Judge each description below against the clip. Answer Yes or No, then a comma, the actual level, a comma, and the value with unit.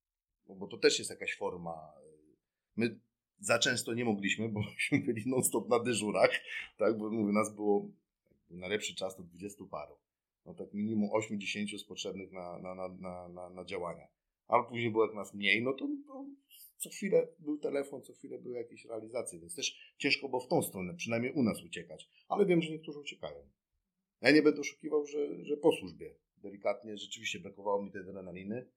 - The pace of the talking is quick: Yes, fast, 175 wpm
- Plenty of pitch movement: Yes, wide, 6.8 semitones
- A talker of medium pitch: No, low, 110 Hz